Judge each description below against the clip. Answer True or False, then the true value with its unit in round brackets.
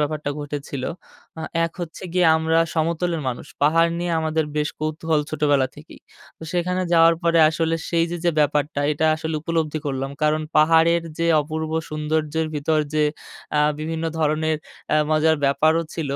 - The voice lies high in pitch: False (155 Hz)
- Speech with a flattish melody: True (1.5 semitones)